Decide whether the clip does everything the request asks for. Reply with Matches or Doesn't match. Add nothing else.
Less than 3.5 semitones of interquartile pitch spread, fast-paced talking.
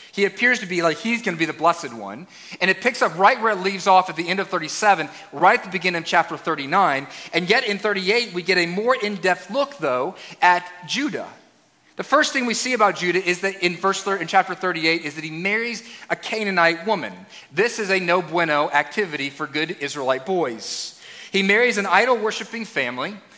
Doesn't match